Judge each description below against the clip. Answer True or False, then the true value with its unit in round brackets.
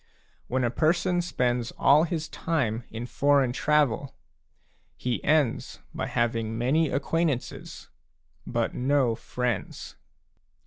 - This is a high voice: False (130 Hz)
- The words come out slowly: True (105 wpm)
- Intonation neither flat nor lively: True (4.3 semitones)